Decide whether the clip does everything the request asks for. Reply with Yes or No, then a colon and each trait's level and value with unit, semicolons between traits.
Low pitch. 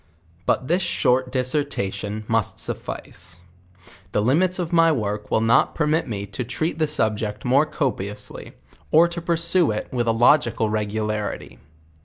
Yes: low, 125 Hz